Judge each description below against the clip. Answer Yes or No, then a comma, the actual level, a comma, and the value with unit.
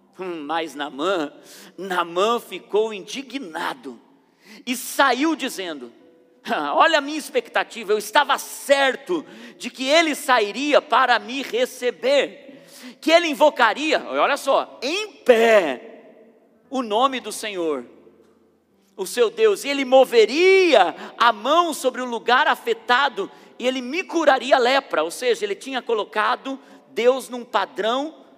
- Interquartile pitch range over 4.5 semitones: Yes, wide, 5.5 semitones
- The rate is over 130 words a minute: No, average, 125 wpm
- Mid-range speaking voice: No, very high, 260 Hz